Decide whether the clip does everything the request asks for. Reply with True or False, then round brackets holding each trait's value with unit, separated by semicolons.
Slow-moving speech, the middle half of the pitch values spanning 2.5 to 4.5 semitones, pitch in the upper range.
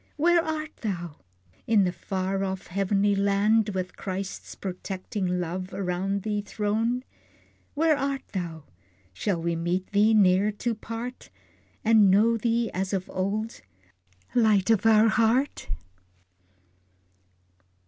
True (120 wpm; 3.3 semitones; 200 Hz)